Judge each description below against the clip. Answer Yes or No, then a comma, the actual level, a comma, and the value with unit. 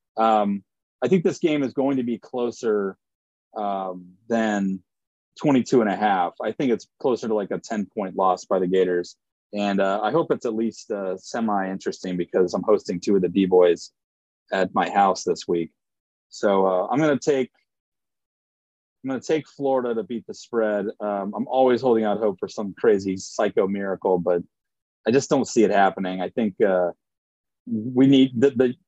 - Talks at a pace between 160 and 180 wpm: No, average, 190 wpm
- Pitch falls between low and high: No, low, 100 Hz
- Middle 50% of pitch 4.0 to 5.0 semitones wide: Yes, average, 4.5 semitones